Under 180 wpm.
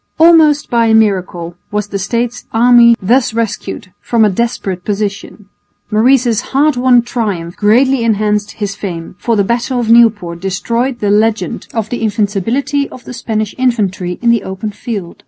Yes: average, 160 wpm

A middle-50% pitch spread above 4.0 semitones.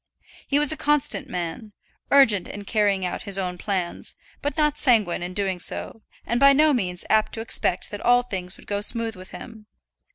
Yes: wide, 5.4 semitones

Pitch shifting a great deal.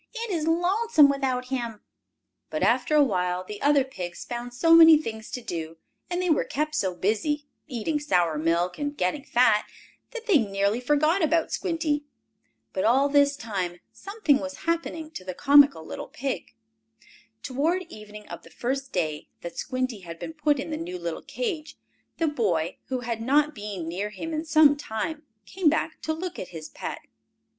Yes: wide, 7.1 semitones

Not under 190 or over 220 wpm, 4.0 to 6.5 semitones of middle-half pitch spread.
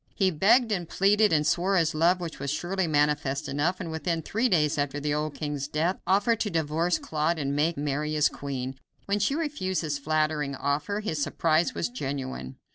Yes: average, 195 wpm; average, 4.3 semitones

